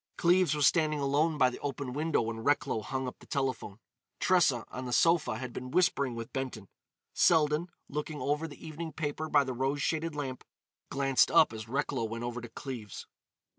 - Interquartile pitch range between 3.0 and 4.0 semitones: Yes, average, 3.7 semitones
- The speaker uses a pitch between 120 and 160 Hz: Yes, medium, 140 Hz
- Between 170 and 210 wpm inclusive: Yes, average, 185 wpm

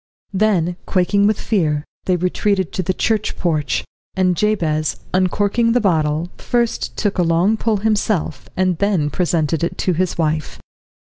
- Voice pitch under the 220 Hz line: Yes, medium, 185 Hz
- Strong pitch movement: No, average, 3.8 semitones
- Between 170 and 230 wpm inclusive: No, average, 150 wpm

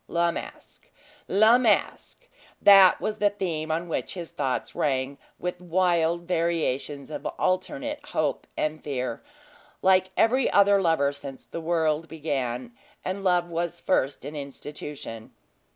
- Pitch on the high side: No, medium, 170 Hz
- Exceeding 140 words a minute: No, slow, 135 wpm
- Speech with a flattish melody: No, average, 4.2 semitones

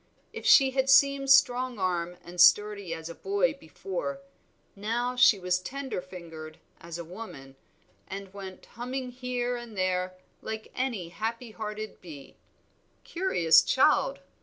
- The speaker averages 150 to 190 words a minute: No, slow, 135 wpm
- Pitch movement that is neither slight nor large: No, wide, 5.8 semitones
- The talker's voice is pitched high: Yes, high, 215 Hz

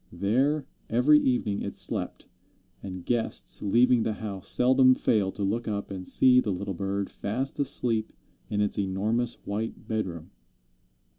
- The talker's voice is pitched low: Yes, low, 110 Hz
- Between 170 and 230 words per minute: No, average, 145 wpm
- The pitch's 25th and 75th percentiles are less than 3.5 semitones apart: No, average, 3.9 semitones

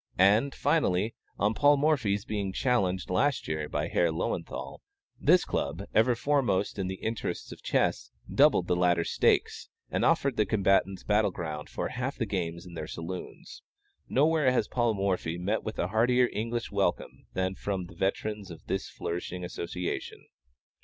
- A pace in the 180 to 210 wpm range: No, average, 160 wpm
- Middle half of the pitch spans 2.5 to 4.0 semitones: No, average, 4.8 semitones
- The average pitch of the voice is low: Yes, low, 100 Hz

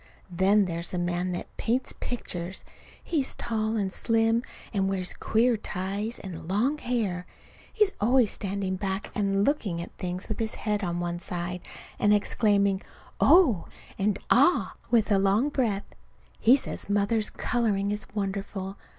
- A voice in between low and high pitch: No, high, 200 Hz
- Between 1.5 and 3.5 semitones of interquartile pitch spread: Yes, average, 3.2 semitones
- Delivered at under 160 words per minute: Yes, average, 150 wpm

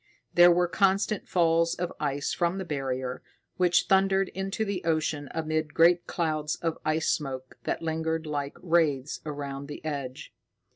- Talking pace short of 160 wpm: Yes, average, 150 wpm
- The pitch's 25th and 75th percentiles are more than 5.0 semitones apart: No, average, 3.3 semitones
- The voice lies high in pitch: No, medium, 160 Hz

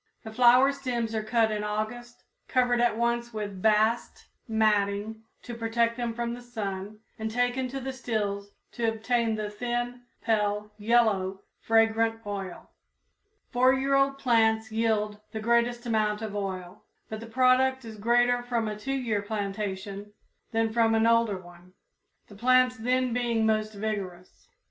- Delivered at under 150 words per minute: No, average, 155 wpm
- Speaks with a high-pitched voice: Yes, high, 225 Hz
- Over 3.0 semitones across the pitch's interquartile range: No, narrow, 2.4 semitones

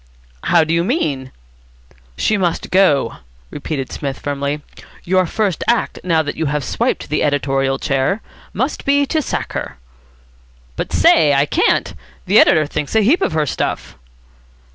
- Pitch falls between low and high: Yes, medium, 155 Hz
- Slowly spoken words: No, average, 155 wpm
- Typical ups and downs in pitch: No, wide, 5.7 semitones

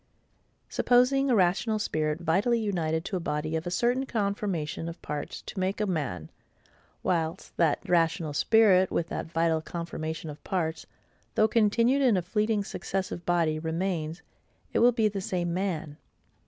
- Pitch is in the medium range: Yes, medium, 175 Hz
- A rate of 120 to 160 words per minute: Yes, average, 155 wpm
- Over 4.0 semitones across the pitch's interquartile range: Yes, average, 4.7 semitones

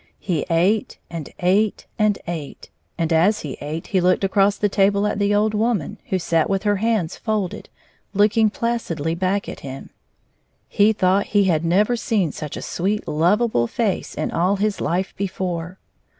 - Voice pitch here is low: No, high, 195 Hz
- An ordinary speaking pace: Yes, average, 170 wpm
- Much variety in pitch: No, average, 3.7 semitones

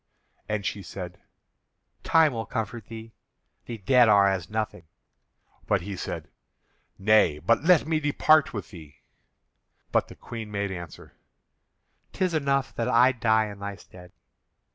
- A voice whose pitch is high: No, low, 110 Hz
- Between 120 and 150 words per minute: Yes, average, 140 wpm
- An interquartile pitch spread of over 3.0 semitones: Yes, average, 4.5 semitones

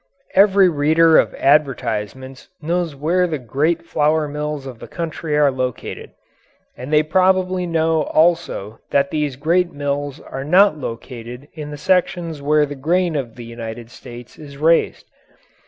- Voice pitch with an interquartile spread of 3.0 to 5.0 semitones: Yes, average, 3.8 semitones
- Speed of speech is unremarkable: Yes, average, 150 wpm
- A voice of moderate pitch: Yes, medium, 150 Hz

